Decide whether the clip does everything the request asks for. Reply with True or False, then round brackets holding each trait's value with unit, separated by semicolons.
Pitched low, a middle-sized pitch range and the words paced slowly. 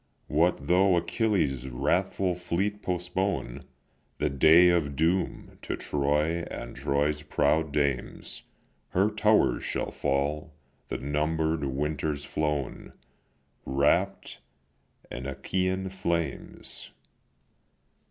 True (80 Hz; 4.0 semitones; 95 wpm)